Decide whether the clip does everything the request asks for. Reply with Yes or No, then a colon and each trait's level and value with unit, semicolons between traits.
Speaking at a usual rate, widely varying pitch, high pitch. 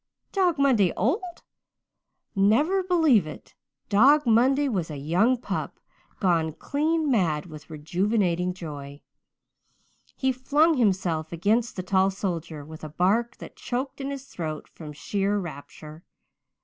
No: slow, 130 wpm; wide, 8.4 semitones; high, 200 Hz